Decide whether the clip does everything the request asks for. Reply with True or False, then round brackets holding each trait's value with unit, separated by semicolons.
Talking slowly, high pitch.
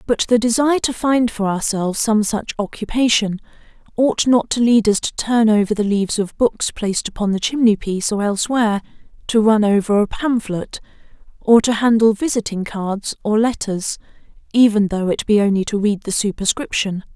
False (175 wpm; 215 Hz)